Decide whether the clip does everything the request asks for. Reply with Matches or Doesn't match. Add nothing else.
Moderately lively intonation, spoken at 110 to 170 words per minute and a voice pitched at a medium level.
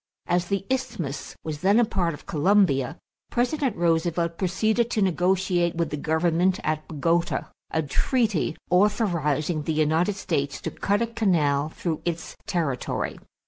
Matches